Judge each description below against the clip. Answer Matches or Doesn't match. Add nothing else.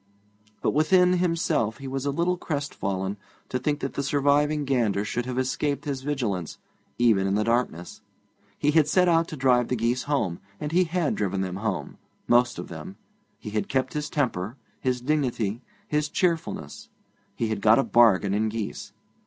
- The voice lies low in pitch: Matches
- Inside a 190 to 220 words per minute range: Doesn't match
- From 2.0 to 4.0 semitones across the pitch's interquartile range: Doesn't match